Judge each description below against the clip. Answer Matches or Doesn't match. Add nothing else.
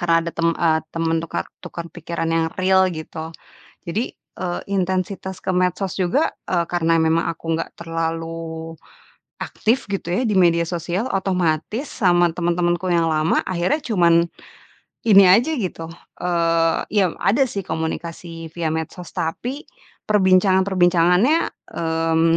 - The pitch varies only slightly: Matches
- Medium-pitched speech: Matches